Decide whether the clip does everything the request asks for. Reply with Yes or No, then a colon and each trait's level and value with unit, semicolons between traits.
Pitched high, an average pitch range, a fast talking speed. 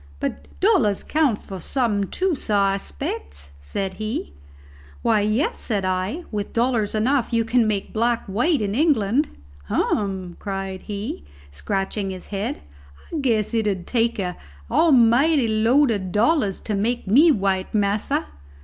No: high, 210 Hz; average, 3.8 semitones; average, 150 wpm